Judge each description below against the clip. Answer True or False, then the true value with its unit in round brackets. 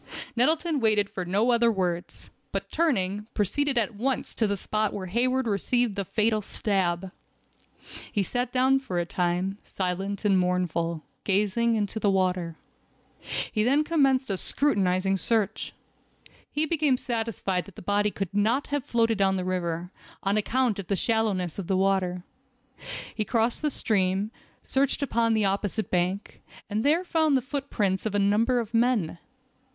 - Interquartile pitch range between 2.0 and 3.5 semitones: False (4.3 semitones)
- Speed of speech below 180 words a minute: True (160 wpm)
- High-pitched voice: True (210 Hz)